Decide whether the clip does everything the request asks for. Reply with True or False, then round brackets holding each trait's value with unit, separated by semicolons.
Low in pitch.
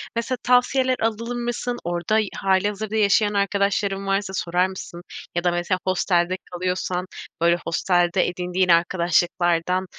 False (190 Hz)